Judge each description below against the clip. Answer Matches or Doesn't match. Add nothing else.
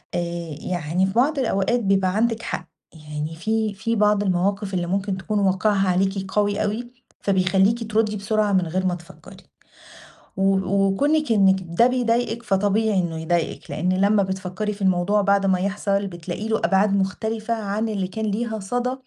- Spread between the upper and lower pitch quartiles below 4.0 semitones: Matches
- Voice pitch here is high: Matches